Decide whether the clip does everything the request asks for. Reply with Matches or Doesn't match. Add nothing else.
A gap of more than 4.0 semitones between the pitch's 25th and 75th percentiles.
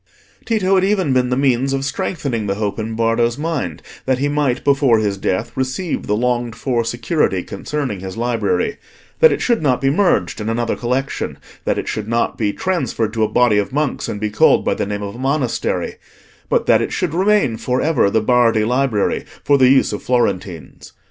Matches